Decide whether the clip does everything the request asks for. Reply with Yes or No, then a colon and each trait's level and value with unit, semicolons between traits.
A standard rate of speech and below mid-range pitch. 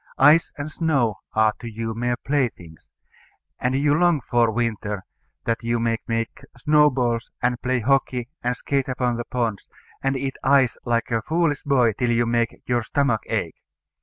Yes: average, 165 wpm; low, 120 Hz